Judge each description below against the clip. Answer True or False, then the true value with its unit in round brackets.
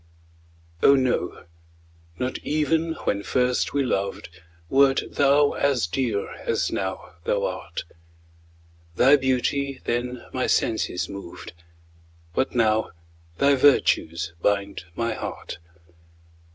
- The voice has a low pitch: True (125 Hz)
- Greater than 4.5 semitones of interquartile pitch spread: True (5.3 semitones)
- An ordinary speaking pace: False (105 wpm)